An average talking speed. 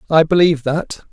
Yes: average, 160 wpm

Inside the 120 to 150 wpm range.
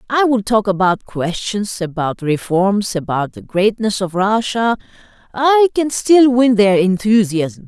Yes: average, 140 wpm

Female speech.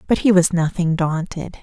Yes: female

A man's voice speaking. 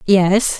No: female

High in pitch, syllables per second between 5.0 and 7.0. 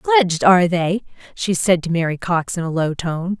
No: medium, 180 Hz; 5.4 syllables/s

